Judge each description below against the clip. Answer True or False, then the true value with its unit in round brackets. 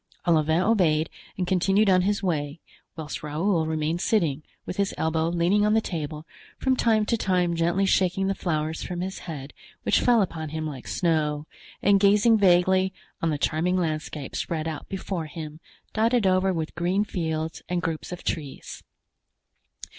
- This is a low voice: False (175 Hz)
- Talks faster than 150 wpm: True (165 wpm)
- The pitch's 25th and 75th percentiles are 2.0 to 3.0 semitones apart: False (3.5 semitones)